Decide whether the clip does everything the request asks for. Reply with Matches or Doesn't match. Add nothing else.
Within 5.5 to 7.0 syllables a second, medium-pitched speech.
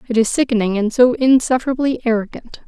Doesn't match